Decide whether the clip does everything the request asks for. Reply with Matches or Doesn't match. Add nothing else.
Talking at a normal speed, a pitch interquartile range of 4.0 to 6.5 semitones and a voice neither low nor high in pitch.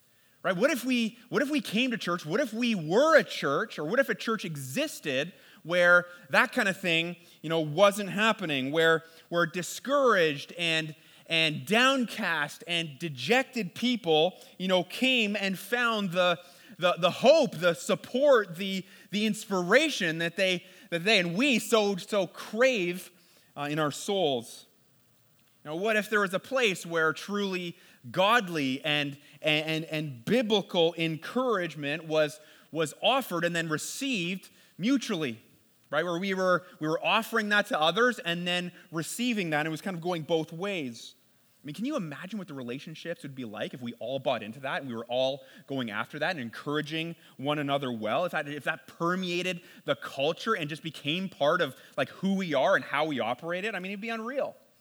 Matches